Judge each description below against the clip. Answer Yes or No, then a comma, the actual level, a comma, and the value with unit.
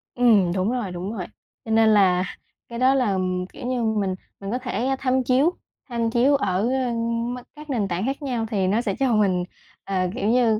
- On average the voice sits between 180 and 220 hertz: No, high, 230 Hz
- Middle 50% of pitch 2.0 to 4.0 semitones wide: No, average, 4.4 semitones